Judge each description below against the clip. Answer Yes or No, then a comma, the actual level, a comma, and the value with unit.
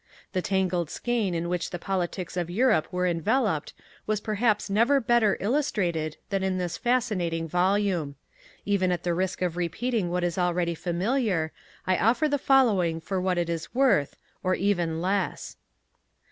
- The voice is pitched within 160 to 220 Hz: Yes, medium, 185 Hz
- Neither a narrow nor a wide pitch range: Yes, average, 3.7 semitones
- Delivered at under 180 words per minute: Yes, average, 160 wpm